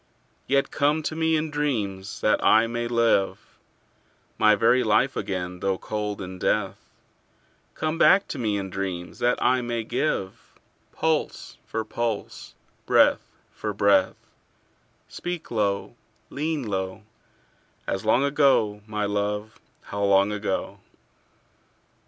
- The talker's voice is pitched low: Yes, low, 110 Hz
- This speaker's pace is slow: Yes, slow, 125 wpm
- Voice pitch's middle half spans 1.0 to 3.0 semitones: No, average, 4.9 semitones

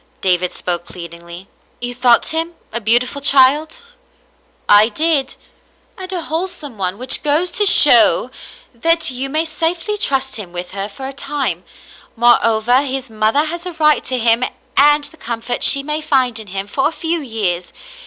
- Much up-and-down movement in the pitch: Yes, wide, 5.9 semitones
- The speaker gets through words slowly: No, average, 180 wpm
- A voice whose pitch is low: No, very high, 260 Hz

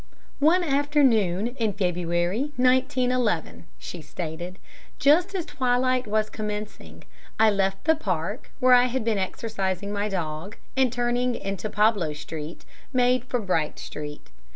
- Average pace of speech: No, slow, 130 wpm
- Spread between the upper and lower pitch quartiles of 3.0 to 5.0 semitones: No, wide, 5.6 semitones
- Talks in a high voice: Yes, high, 215 Hz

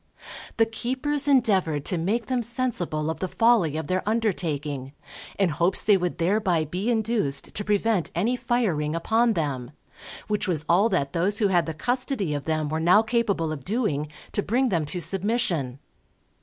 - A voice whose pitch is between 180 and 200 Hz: Yes, high, 190 Hz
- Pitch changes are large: Yes, wide, 6.2 semitones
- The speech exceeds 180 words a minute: No, average, 170 wpm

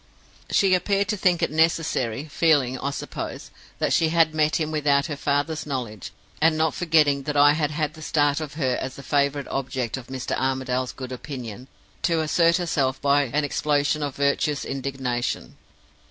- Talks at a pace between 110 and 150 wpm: No, average, 175 wpm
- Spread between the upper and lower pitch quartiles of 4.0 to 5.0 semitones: No, average, 2.9 semitones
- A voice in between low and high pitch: Yes, medium, 145 Hz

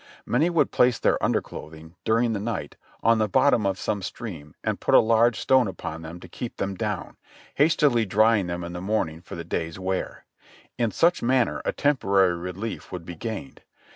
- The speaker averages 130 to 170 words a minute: No, average, 190 wpm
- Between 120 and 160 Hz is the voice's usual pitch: No, low, 105 Hz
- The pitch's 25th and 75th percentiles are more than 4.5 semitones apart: Yes, average, 5.1 semitones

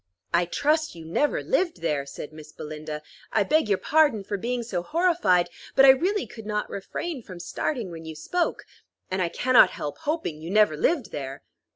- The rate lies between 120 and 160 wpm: No, average, 190 wpm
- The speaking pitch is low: No, high, 205 Hz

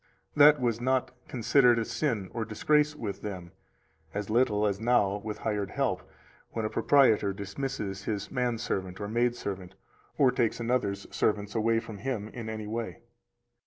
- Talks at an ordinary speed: Yes, average, 160 wpm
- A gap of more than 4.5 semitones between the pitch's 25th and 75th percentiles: No, average, 3.2 semitones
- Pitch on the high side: No, low, 110 Hz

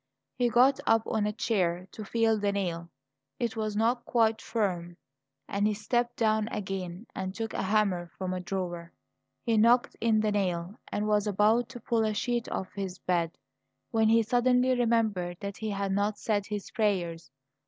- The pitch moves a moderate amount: Yes, average, 3.2 semitones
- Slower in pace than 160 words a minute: No, average, 180 wpm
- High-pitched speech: Yes, high, 210 Hz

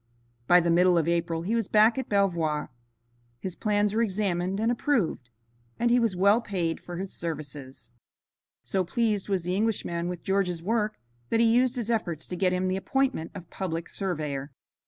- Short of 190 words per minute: Yes, average, 180 wpm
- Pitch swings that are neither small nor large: Yes, average, 4.2 semitones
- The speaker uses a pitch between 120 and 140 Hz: No, medium, 185 Hz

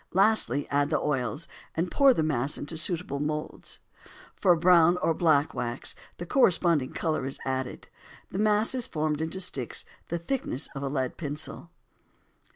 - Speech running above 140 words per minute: Yes, average, 160 wpm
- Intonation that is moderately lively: Yes, average, 4.0 semitones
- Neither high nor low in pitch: Yes, medium, 160 Hz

